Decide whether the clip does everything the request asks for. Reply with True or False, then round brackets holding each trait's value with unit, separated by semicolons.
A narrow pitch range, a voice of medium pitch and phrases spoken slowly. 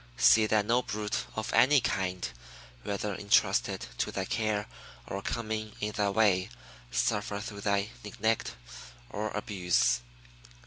False (1.5 semitones; 105 Hz; 130 wpm)